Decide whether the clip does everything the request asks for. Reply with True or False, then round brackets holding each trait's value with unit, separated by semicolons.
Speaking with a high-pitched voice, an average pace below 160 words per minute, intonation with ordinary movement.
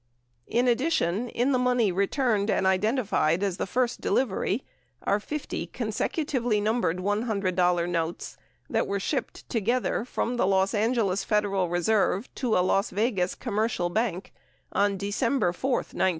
True (210 Hz; 140 wpm; 4.3 semitones)